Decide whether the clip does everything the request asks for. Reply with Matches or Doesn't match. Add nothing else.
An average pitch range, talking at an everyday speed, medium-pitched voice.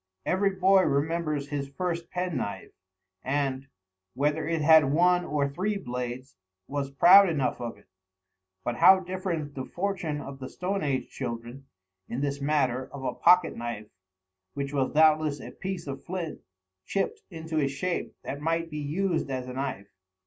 Matches